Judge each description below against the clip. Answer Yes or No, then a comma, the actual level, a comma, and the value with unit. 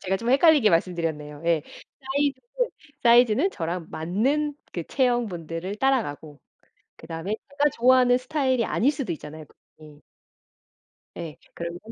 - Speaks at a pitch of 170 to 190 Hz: No, high, 215 Hz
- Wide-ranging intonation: Yes, wide, 8.2 semitones